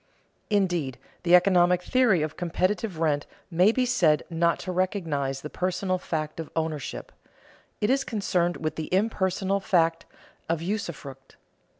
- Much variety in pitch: No, average, 3.5 semitones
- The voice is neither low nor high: Yes, medium, 175 Hz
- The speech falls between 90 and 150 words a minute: Yes, slow, 135 wpm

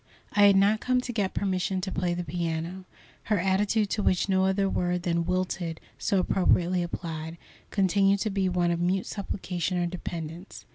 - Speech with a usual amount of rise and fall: No, narrow, 2.1 semitones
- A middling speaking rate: Yes, average, 180 wpm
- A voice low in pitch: No, medium, 185 Hz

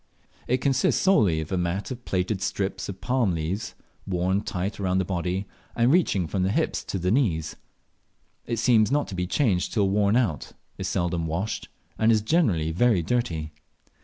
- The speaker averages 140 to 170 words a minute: No, average, 180 wpm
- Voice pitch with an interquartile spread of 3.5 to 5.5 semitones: Yes, average, 4.6 semitones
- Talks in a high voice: No, very low, 95 Hz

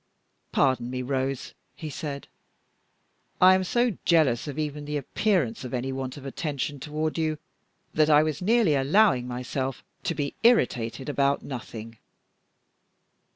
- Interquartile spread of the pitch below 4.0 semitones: Yes, average, 3.3 semitones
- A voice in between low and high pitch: Yes, medium, 145 Hz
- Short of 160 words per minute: Yes, average, 140 wpm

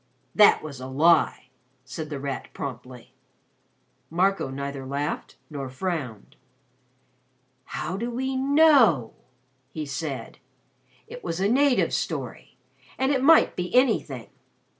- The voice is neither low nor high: Yes, medium, 160 Hz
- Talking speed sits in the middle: No, slow, 120 wpm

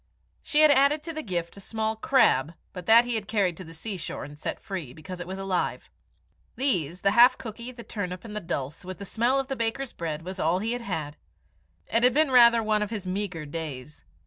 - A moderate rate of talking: No, fast, 225 wpm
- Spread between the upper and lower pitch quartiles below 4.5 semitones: No, wide, 5.5 semitones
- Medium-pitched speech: No, high, 200 Hz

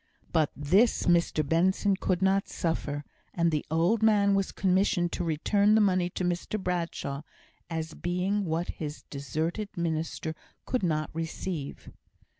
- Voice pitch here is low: No, medium, 175 Hz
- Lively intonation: No, average, 3.4 semitones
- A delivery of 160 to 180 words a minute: No, average, 140 wpm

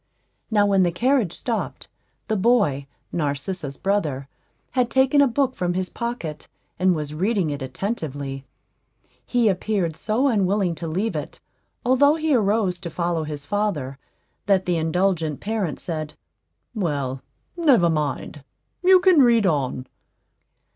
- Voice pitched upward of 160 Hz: Yes, medium, 185 Hz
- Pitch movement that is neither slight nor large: No, wide, 6.8 semitones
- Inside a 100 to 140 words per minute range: Yes, slow, 135 wpm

